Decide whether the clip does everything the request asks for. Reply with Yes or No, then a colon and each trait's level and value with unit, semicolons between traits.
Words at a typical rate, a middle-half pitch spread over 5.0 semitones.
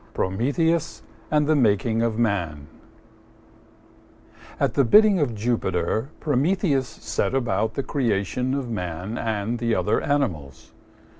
No: slow, 120 wpm; wide, 5.6 semitones